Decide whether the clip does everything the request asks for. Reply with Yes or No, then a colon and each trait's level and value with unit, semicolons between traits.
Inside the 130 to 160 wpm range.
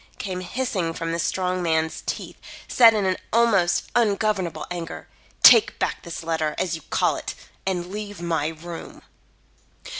Yes: average, 145 wpm